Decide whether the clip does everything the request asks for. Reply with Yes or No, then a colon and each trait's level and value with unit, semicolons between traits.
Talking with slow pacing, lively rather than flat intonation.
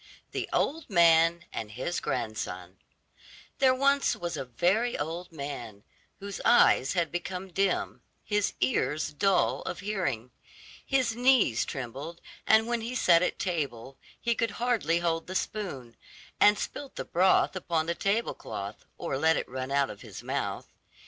No: average, 155 wpm; wide, 7.3 semitones